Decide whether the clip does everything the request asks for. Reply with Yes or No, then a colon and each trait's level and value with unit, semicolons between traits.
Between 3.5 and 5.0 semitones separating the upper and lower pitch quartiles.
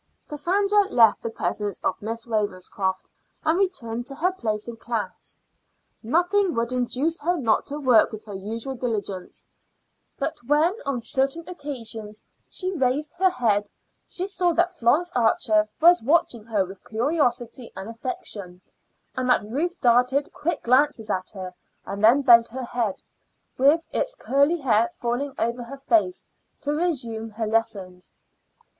No: wide, 5.5 semitones